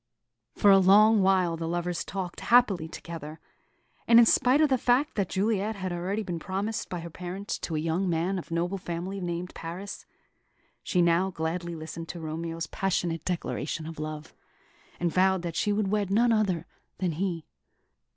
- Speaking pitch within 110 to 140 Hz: No, medium, 180 Hz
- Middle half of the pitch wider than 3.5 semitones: No, average, 3.0 semitones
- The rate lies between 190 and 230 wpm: No, average, 175 wpm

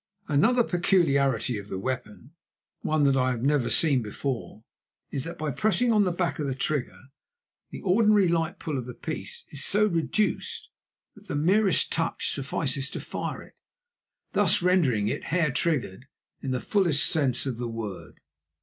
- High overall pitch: No, medium, 145 Hz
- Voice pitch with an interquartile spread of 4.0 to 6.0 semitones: Yes, wide, 5.5 semitones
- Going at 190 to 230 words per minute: No, average, 170 wpm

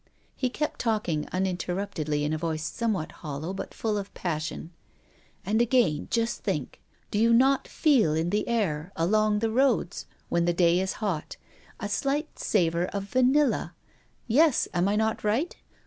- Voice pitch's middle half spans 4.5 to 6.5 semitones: Yes, wide, 5.4 semitones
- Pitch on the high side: Yes, high, 205 Hz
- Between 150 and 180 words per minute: Yes, average, 160 wpm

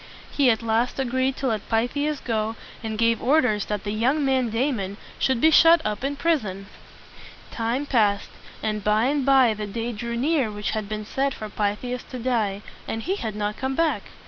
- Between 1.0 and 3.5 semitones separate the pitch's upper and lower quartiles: No, average, 4.0 semitones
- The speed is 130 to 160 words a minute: No, average, 200 wpm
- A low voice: No, high, 230 Hz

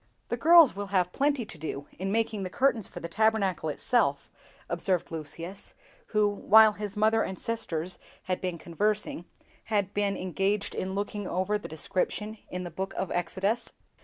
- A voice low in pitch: No, high, 200 Hz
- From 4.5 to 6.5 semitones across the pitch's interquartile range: No, average, 3.1 semitones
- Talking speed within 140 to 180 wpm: Yes, average, 165 wpm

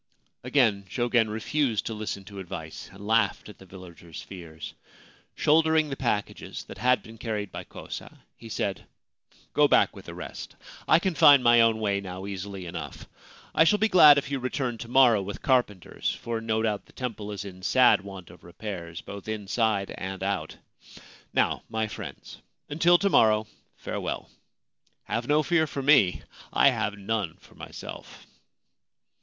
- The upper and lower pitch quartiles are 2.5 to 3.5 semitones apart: No, average, 4.5 semitones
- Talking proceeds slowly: No, average, 170 wpm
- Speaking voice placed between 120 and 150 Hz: No, low, 110 Hz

